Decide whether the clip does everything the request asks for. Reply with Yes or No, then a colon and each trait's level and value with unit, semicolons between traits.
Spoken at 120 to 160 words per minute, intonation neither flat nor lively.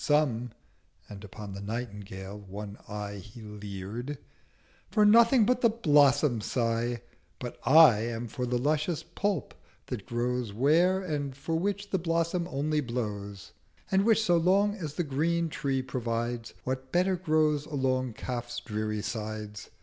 No: average, 140 wpm; wide, 7.0 semitones